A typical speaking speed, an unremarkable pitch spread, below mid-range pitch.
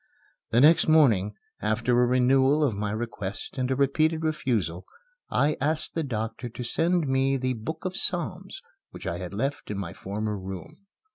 No: average, 170 wpm; wide, 5.8 semitones; low, 130 Hz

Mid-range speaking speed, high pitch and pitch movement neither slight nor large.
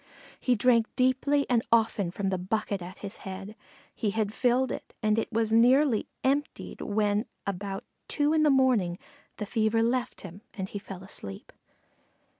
Yes: average, 165 wpm; high, 220 Hz; average, 4.2 semitones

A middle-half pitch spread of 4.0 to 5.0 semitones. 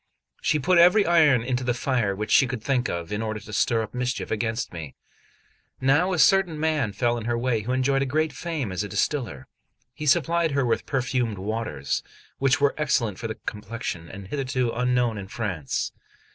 Yes: average, 4.5 semitones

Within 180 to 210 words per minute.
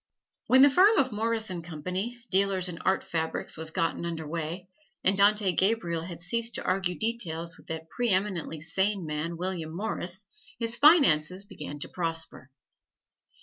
No: average, 160 wpm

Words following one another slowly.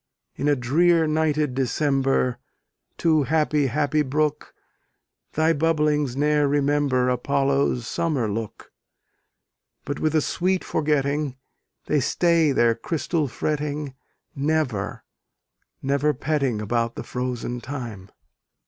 Yes: slow, 105 wpm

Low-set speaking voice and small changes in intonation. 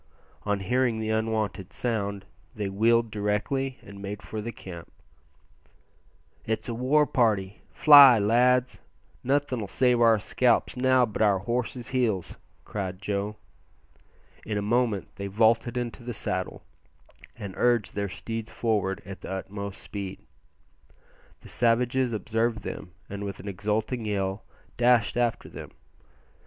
No: low, 110 Hz; average, 3.2 semitones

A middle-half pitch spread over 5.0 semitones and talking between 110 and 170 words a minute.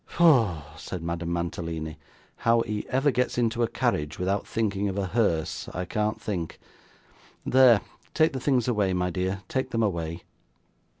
Yes: wide, 5.4 semitones; average, 160 wpm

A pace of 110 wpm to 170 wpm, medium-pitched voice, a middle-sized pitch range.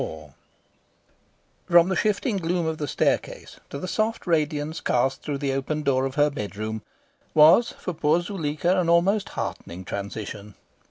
Yes: average, 160 wpm; medium, 150 Hz; average, 4.8 semitones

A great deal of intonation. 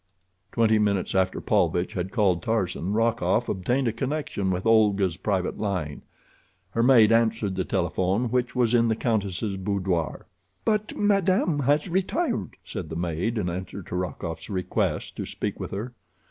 No: average, 4.3 semitones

